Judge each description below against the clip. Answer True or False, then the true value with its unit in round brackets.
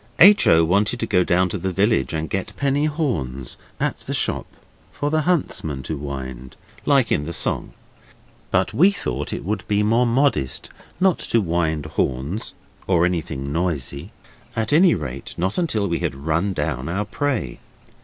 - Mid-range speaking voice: False (90 Hz)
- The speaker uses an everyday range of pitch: False (8.0 semitones)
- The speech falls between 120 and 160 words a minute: False (170 wpm)